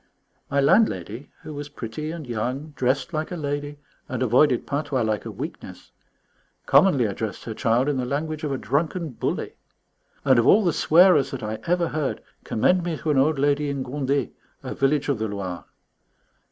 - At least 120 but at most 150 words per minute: No, average, 180 wpm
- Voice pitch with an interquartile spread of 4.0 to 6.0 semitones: No, average, 3.6 semitones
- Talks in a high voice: No, medium, 140 Hz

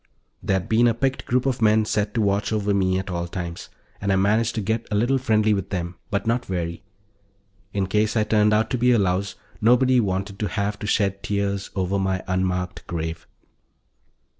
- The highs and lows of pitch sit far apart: No, average, 2.7 semitones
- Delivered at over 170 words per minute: Yes, average, 200 wpm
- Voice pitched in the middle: No, low, 100 Hz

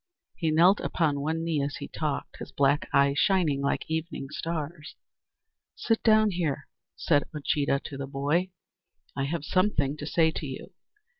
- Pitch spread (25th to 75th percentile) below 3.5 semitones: Yes, average, 3.1 semitones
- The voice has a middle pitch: Yes, medium, 155 Hz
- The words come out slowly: No, average, 160 wpm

